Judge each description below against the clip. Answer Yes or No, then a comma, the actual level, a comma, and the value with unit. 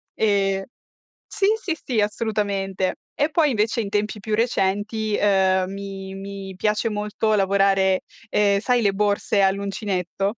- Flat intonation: Yes, narrow, 1.8 semitones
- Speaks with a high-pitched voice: Yes, high, 200 Hz